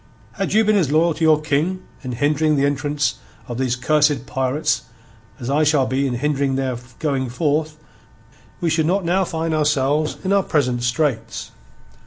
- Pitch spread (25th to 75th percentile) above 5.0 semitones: No, average, 3.1 semitones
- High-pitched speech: No, medium, 150 Hz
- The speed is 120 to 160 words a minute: No, average, 180 wpm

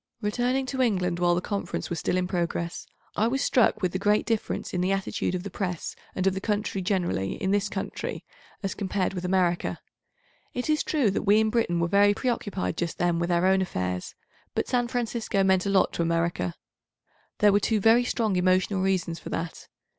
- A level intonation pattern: No, average, 3.2 semitones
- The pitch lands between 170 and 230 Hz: Yes, high, 190 Hz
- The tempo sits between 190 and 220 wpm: Yes, average, 200 wpm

